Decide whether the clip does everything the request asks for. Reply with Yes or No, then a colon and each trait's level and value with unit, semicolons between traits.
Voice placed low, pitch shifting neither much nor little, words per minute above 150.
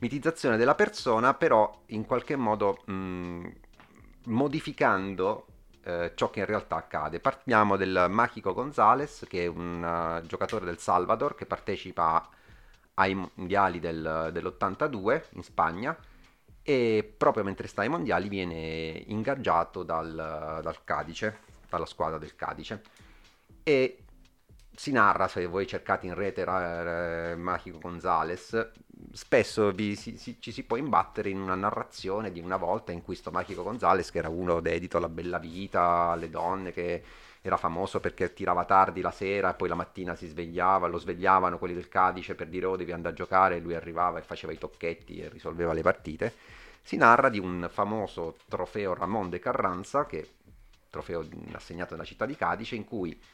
Yes: very low, 90 Hz; average, 3.0 semitones; average, 160 wpm